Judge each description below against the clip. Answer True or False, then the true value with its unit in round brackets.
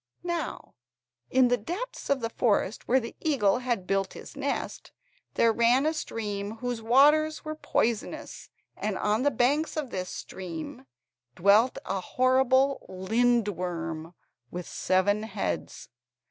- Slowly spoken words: True (130 wpm)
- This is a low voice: False (230 Hz)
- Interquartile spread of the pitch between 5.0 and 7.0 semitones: True (5.3 semitones)